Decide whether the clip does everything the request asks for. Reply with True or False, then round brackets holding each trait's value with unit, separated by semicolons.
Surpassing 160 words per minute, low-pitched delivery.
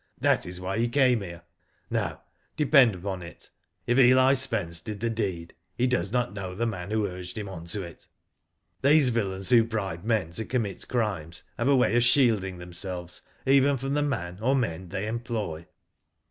True (185 wpm; 105 Hz)